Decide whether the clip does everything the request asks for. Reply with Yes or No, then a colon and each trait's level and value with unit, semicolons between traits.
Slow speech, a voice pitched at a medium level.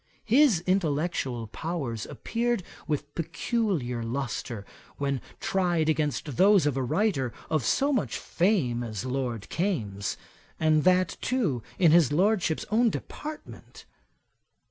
Yes: slow, 120 wpm; medium, 155 Hz